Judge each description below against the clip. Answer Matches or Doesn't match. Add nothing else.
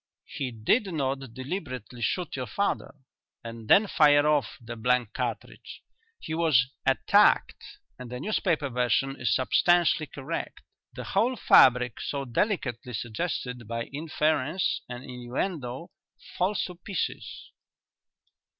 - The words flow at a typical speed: Doesn't match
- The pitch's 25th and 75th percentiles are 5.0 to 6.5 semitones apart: Matches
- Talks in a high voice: Doesn't match